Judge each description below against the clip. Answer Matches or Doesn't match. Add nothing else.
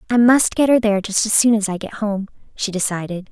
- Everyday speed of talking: Doesn't match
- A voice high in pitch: Matches